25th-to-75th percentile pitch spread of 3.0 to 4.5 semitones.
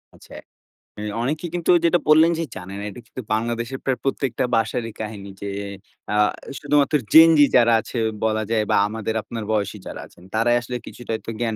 Yes: average, 3.8 semitones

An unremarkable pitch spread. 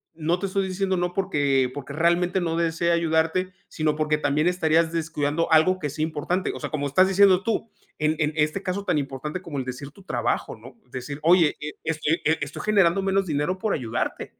Yes: average, 3.6 semitones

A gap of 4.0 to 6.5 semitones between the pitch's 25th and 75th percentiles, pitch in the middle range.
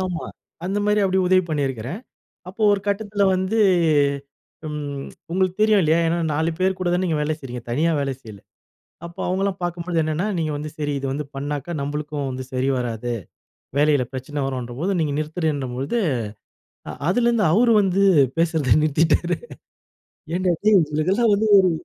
Yes: average, 4.7 semitones; medium, 160 Hz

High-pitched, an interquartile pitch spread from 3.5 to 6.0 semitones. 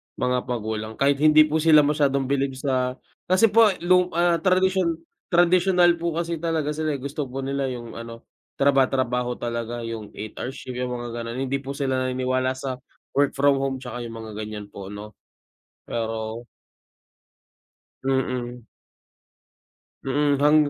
No: low, 135 Hz; average, 4.1 semitones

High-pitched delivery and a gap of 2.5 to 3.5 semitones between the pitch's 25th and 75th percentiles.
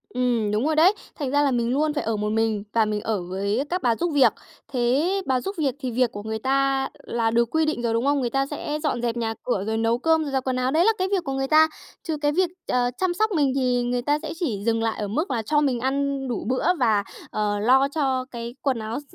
No: very high, 255 Hz; average, 4.3 semitones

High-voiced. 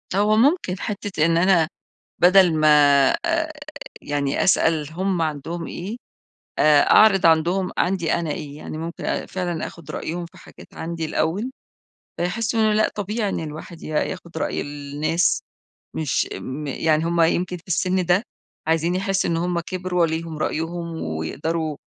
No: medium, 170 Hz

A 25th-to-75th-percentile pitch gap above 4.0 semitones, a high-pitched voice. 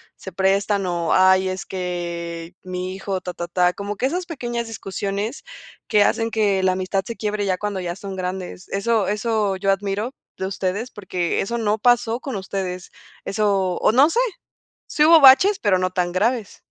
No: average, 3.2 semitones; high, 195 Hz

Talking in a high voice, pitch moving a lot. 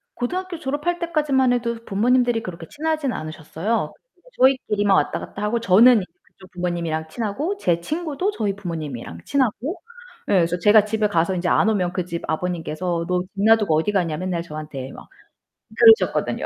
Yes: high, 205 Hz; wide, 7.0 semitones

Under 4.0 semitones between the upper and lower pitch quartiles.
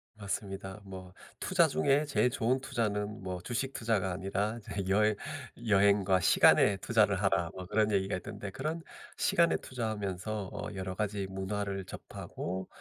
Yes: narrow, 2.6 semitones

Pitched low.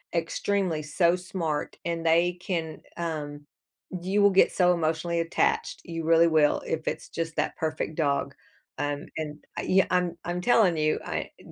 No: medium, 165 Hz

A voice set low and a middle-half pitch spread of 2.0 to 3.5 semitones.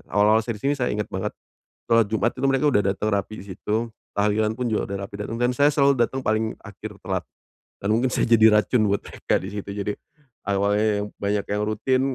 Yes: low, 110 Hz; narrow, 2.5 semitones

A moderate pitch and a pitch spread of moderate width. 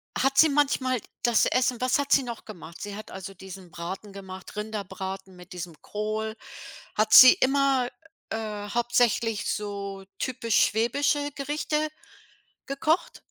No: high, 220 Hz; average, 4.9 semitones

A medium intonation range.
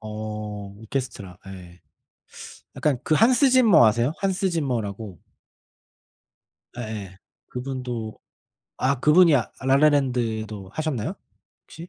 No: wide, 6.0 semitones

